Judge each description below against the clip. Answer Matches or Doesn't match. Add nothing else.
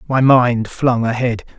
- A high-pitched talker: Doesn't match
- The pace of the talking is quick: Doesn't match